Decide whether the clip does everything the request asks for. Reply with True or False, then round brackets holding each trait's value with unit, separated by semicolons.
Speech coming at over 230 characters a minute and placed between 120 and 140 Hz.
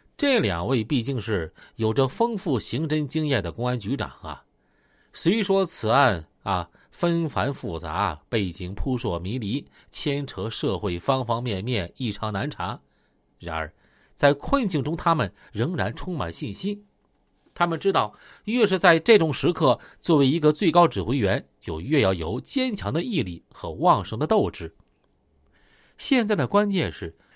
False (225 characters per minute; 135 Hz)